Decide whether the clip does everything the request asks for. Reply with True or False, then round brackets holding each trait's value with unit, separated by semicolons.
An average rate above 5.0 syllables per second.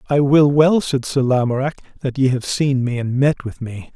False (4.9 syllables/s)